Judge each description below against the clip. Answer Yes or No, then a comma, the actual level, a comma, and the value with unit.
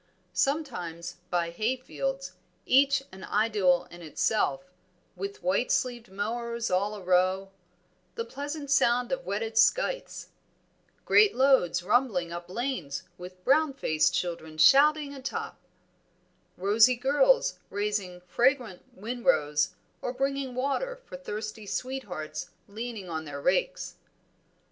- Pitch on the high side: Yes, high, 220 Hz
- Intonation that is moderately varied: No, wide, 6.9 semitones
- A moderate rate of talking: No, slow, 110 wpm